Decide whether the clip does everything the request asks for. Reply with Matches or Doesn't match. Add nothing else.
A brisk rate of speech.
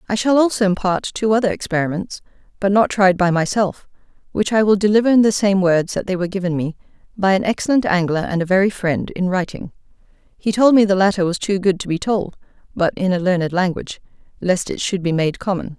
Matches